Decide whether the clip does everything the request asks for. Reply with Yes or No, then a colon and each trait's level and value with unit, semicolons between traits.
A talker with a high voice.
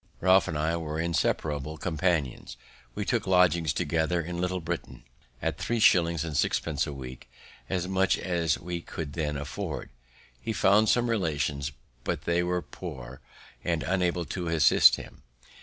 No: very low, 85 Hz